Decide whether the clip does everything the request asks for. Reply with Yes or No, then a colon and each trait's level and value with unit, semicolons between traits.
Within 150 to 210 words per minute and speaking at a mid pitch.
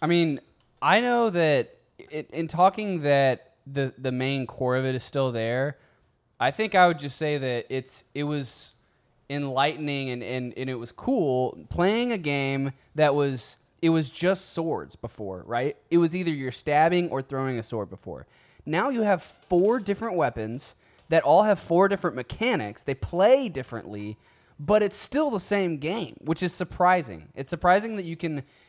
Yes: average, 180 wpm; medium, 145 Hz